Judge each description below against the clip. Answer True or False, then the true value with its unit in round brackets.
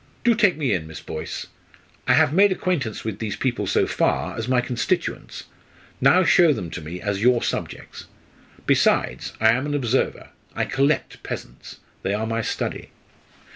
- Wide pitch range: True (5.7 semitones)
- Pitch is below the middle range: True (125 Hz)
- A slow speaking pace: False (170 wpm)